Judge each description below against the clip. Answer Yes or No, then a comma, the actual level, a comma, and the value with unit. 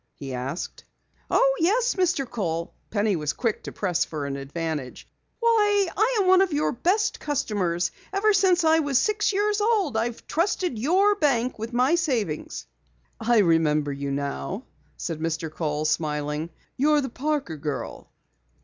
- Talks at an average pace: Yes, average, 155 wpm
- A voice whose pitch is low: No, high, 240 Hz